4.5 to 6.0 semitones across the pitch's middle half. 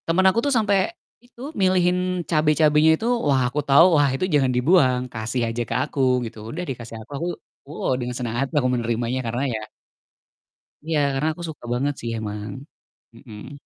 Yes: average, 5.0 semitones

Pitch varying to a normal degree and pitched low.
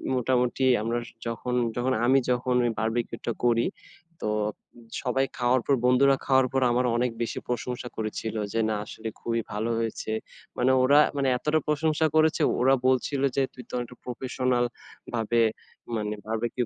No: narrow, 2.1 semitones; low, 125 Hz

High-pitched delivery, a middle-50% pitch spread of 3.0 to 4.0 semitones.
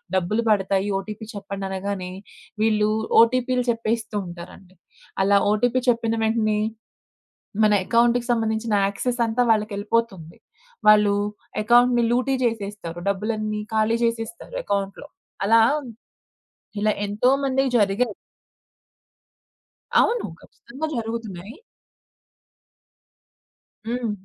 No: high, 220 Hz; narrow, 2.6 semitones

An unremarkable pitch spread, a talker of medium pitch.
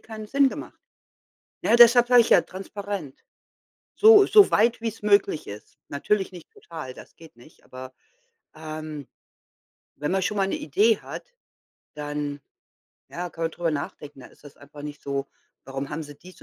No: wide, 6.4 semitones; medium, 165 Hz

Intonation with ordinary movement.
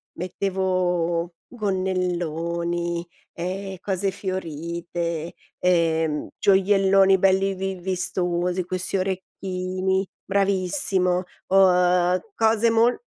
No: narrow, 1.8 semitones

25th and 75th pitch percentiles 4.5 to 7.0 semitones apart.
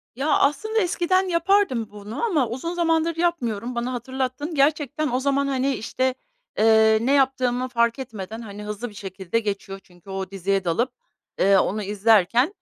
Yes: wide, 5.4 semitones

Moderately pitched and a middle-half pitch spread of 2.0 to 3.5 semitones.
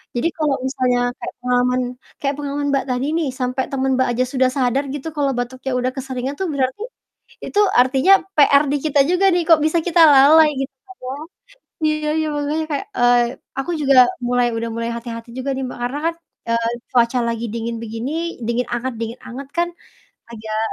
No: very high, 260 Hz; average, 3.0 semitones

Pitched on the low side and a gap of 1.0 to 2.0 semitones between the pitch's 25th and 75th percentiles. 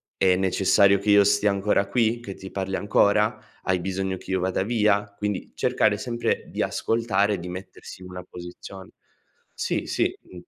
Yes: low, 100 Hz; narrow, 1.7 semitones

